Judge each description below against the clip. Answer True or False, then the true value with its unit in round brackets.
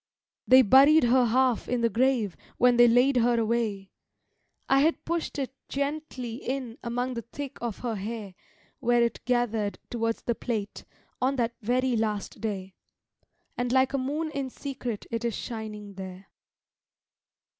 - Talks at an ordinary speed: True (155 wpm)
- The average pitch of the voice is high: True (240 Hz)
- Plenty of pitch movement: False (2.7 semitones)